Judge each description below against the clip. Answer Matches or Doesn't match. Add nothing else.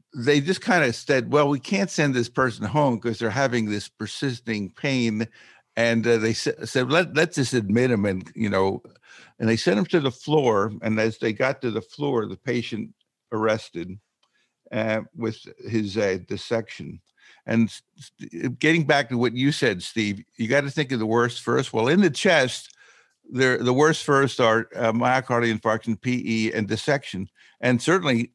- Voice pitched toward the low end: Matches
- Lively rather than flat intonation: Doesn't match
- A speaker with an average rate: Matches